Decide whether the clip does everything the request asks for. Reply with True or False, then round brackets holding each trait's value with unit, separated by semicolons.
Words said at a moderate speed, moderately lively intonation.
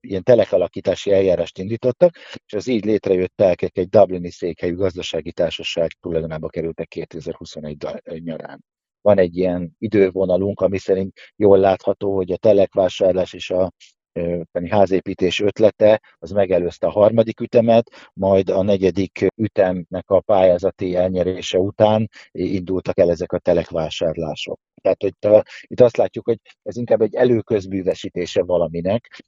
True (130 wpm; 3.1 semitones)